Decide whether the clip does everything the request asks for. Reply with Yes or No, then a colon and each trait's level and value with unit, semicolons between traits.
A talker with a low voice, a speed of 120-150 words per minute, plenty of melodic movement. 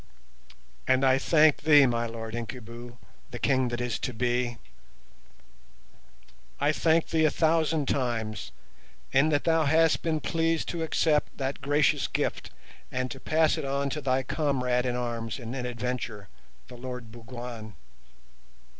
No: low, 130 Hz; average, 140 wpm; average, 4.0 semitones